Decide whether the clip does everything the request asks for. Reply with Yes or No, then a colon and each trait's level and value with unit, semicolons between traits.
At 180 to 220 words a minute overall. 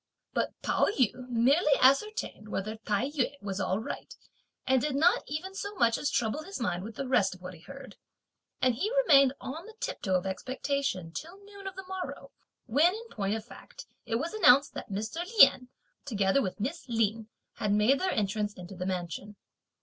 Yes: average, 190 wpm